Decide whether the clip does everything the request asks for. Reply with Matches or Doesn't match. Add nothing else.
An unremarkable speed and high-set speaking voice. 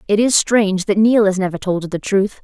Doesn't match